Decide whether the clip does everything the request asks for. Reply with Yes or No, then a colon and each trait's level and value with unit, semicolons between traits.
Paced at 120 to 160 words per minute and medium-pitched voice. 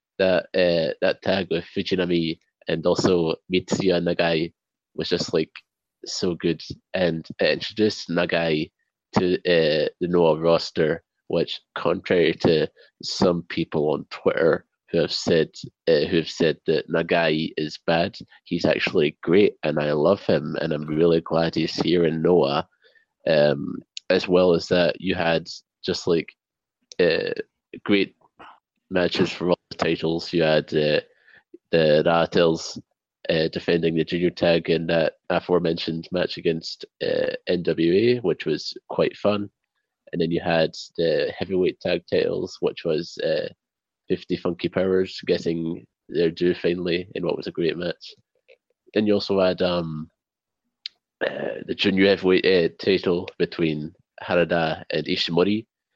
No: average, 140 wpm; very low, 90 Hz